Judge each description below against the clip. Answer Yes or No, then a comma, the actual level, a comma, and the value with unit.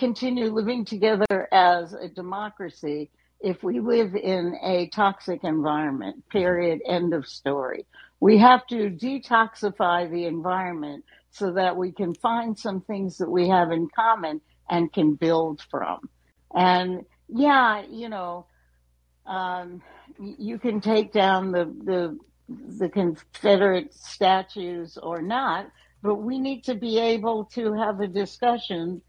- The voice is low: No, high, 190 Hz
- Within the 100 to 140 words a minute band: Yes, slow, 135 wpm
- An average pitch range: Yes, average, 4.5 semitones